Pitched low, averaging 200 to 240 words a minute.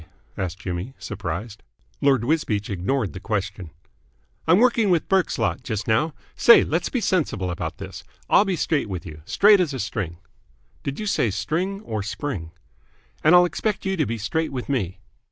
No: low, 130 Hz; average, 175 wpm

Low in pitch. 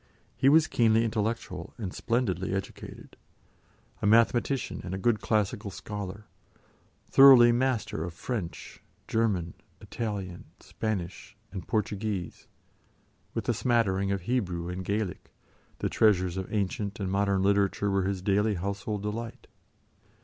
Yes: low, 100 Hz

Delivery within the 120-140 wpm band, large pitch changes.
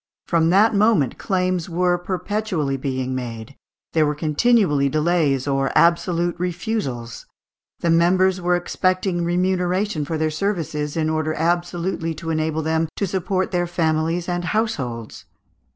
No: slow, 135 wpm; average, 3.1 semitones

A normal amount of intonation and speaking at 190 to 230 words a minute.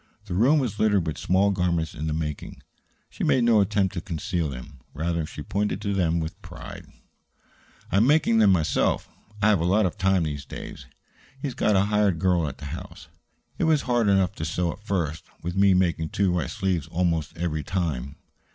Yes: average, 4.0 semitones; average, 200 wpm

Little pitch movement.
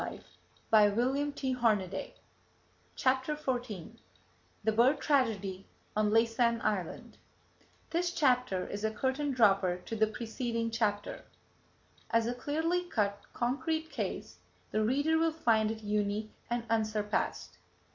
No: average, 3.8 semitones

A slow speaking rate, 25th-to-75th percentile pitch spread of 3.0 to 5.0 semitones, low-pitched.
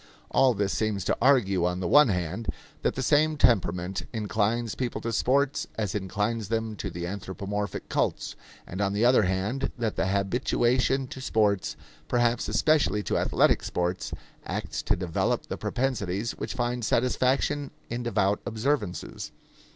No: average, 150 wpm; average, 4.2 semitones; low, 110 Hz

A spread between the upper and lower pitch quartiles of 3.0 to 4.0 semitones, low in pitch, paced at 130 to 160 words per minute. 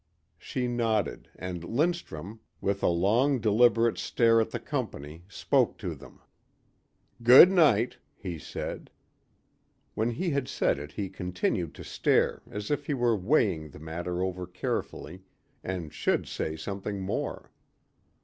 No: wide, 5.4 semitones; low, 100 Hz; average, 140 wpm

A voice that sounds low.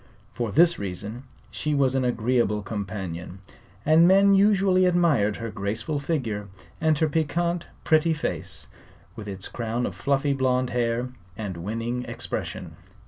Yes: low, 125 Hz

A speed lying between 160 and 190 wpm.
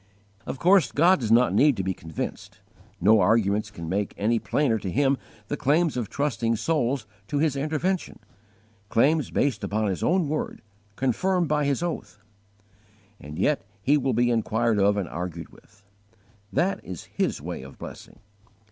Yes: average, 165 wpm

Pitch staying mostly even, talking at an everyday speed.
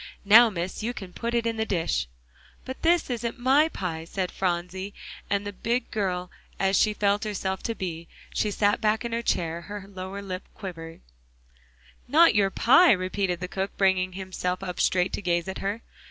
No: average, 3.3 semitones; average, 185 wpm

